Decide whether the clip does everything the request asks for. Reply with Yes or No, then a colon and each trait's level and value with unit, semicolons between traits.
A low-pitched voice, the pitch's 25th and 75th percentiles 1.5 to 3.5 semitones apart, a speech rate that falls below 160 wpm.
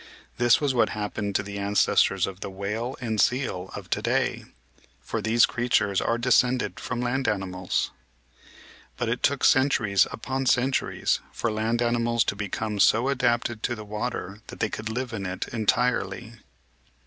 No: low, 115 Hz; average, 3.2 semitones; average, 165 wpm